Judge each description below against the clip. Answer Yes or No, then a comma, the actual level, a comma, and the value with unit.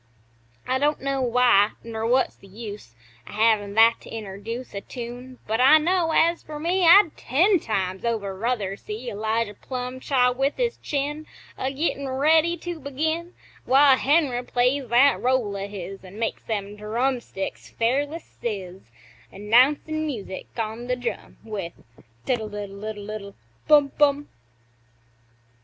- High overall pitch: Yes, high, 245 Hz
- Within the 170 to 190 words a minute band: No, average, 145 wpm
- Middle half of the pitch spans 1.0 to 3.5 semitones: No, average, 5.2 semitones